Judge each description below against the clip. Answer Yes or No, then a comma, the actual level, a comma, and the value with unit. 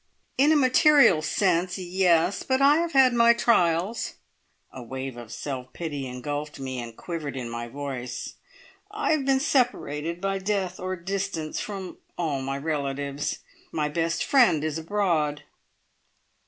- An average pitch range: No, wide, 6.4 semitones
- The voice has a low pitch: No, medium, 165 Hz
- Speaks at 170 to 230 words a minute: No, average, 145 wpm